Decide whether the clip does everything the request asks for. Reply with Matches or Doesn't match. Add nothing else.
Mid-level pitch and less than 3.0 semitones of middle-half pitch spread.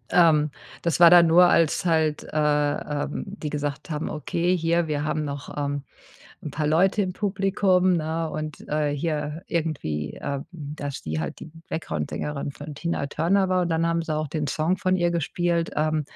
Matches